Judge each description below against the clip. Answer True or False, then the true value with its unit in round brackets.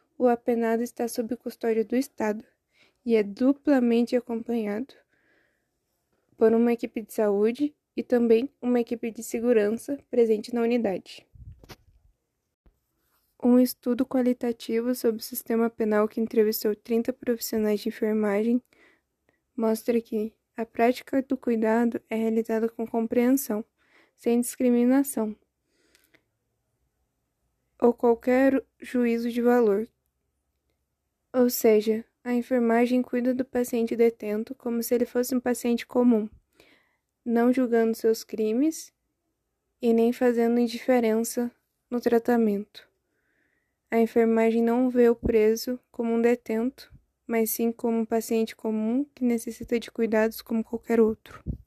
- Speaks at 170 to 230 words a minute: False (120 wpm)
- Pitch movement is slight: True (1.6 semitones)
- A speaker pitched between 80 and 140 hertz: False (235 Hz)